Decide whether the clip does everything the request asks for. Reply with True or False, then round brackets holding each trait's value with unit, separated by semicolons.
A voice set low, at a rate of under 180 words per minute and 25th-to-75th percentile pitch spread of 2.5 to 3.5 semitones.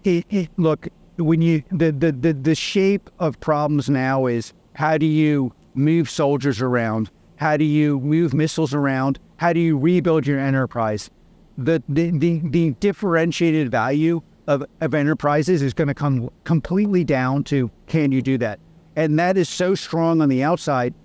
False (155 Hz; 170 wpm; 3.1 semitones)